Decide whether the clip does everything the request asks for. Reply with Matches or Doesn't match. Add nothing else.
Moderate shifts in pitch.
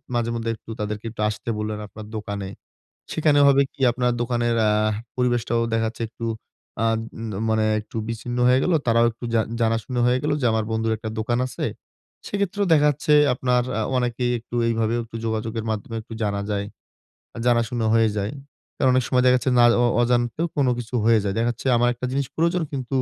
Doesn't match